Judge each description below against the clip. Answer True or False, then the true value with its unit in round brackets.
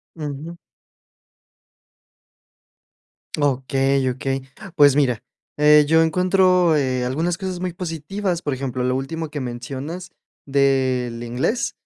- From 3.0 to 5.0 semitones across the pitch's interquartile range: True (4.2 semitones)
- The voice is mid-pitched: True (145 Hz)